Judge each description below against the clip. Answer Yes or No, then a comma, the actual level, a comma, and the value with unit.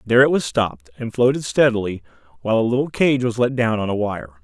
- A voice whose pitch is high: No, low, 115 Hz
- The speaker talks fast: Yes, fast, 230 wpm